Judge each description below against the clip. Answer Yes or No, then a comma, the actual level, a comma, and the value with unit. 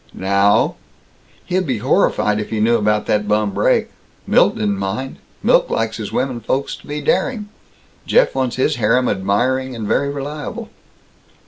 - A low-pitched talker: Yes, low, 115 Hz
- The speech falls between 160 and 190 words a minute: No, average, 150 wpm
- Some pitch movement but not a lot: Yes, average, 4.5 semitones